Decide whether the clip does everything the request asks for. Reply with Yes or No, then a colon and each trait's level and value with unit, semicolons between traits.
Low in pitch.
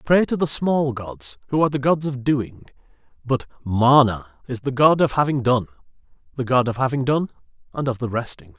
Yes: low, 130 Hz